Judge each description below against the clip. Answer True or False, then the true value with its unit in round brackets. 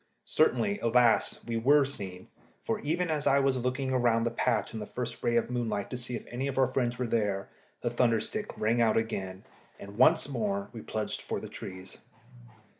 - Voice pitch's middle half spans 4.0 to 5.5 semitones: False (3.0 semitones)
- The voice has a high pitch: False (120 Hz)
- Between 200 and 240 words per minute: True (205 wpm)